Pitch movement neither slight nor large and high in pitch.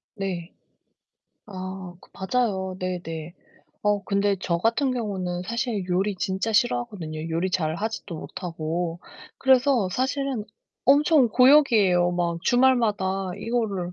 Yes: average, 5.0 semitones; high, 195 Hz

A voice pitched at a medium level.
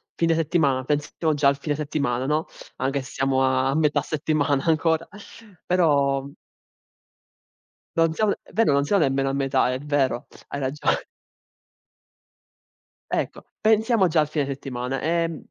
Yes: medium, 145 Hz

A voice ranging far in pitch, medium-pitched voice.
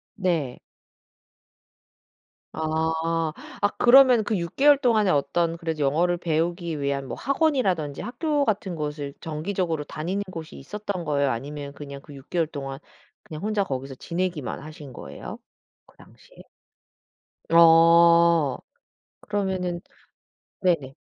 No: average, 4.3 semitones; medium, 165 Hz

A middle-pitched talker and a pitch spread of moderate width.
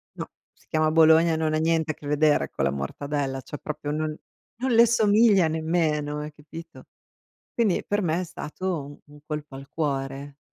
No: medium, 155 Hz; narrow, 2.2 semitones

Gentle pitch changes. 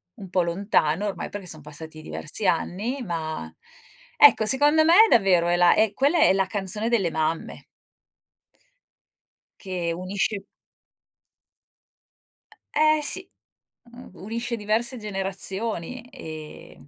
No: wide, 5.7 semitones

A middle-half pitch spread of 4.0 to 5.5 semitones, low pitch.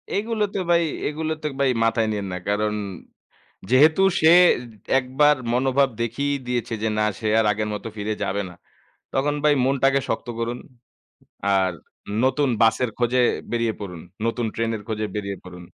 Yes: average, 4.6 semitones; low, 120 Hz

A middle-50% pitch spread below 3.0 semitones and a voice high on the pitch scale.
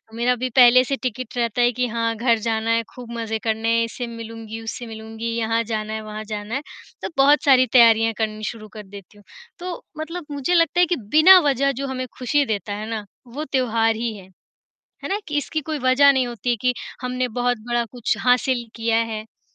Yes: narrow, 2.5 semitones; high, 235 Hz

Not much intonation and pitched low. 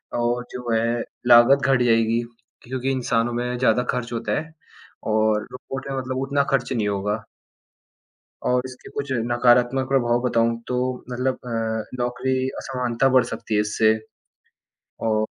Yes: narrow, 2.0 semitones; low, 120 Hz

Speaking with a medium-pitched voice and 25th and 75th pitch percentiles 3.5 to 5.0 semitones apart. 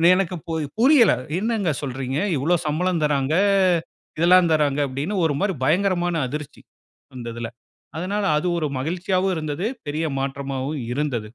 Yes: medium, 155 Hz; average, 4.6 semitones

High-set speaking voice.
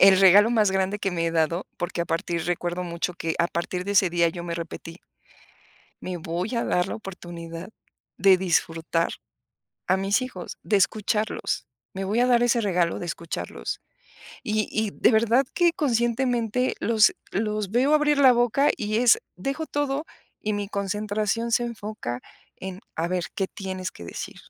Yes: high, 195 Hz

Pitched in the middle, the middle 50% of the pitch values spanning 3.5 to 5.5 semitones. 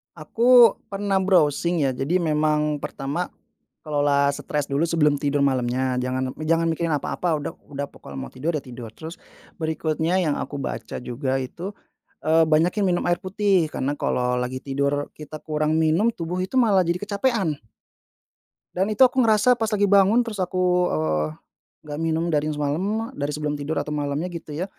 Yes: medium, 155 Hz; average, 4.3 semitones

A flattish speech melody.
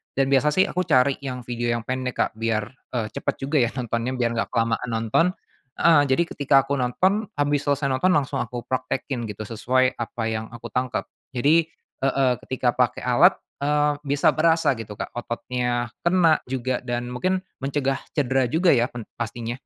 No: average, 3.2 semitones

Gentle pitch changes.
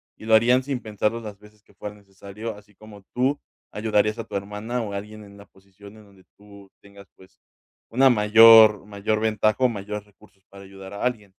Yes: narrow, 1.6 semitones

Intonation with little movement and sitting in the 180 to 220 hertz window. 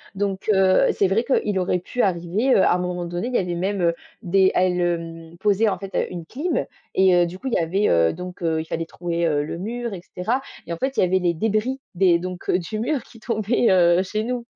No: average, 3.7 semitones; medium, 185 Hz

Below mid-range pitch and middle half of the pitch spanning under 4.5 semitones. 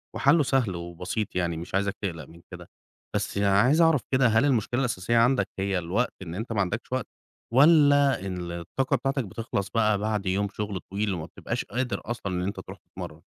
No: low, 105 Hz; wide, 5.4 semitones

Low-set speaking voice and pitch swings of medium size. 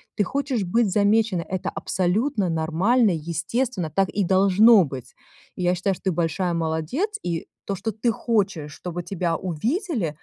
No: high, 190 Hz; average, 4.8 semitones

